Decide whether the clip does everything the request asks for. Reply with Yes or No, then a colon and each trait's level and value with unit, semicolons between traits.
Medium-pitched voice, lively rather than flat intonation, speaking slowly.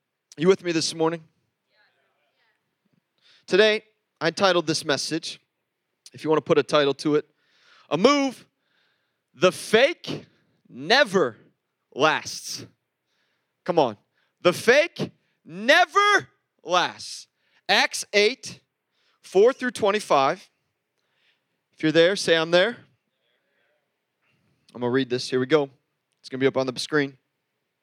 Yes: medium, 165 Hz; wide, 6.3 semitones; slow, 125 wpm